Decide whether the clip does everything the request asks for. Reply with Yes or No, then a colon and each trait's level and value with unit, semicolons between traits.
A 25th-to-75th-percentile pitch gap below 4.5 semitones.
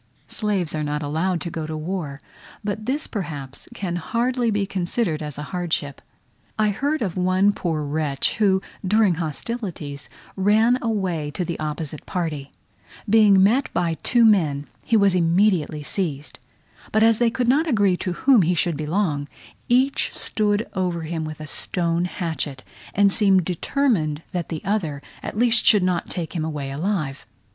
No: average, 5.3 semitones